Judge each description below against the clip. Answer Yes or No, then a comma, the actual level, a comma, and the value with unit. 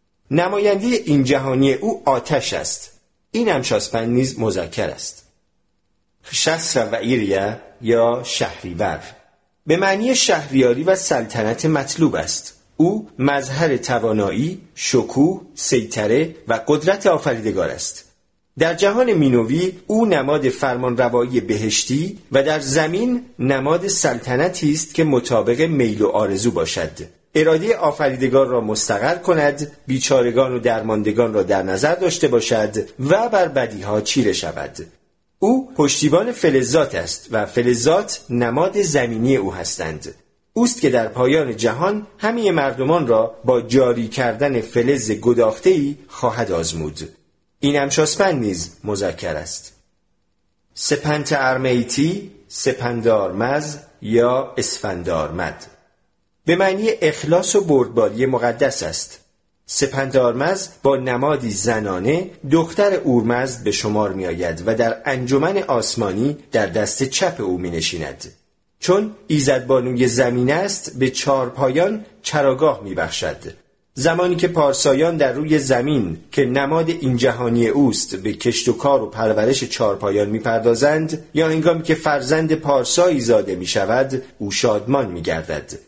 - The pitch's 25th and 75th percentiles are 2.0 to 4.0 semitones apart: No, average, 5.0 semitones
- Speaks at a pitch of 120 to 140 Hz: Yes, low, 135 Hz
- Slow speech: No, average, 120 wpm